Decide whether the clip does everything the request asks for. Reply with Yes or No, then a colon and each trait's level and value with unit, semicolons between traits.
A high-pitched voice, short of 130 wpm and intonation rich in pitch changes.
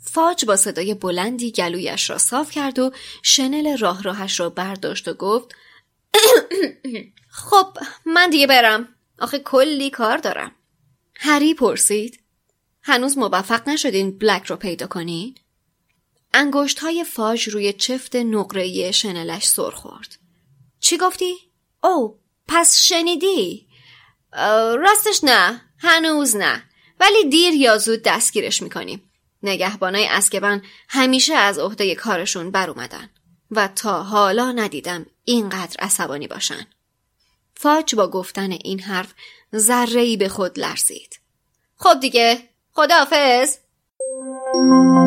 Yes: high, 235 Hz; average, 110 wpm; wide, 7.0 semitones